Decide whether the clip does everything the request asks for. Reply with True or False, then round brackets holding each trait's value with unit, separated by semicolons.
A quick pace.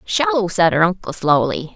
False (170 wpm)